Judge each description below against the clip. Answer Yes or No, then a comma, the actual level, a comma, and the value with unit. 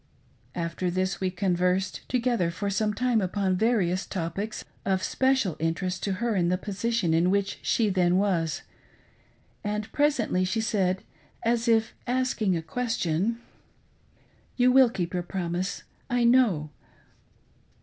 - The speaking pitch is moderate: No, high, 195 Hz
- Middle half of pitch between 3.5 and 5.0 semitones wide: Yes, average, 4.3 semitones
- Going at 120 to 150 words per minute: Yes, average, 140 wpm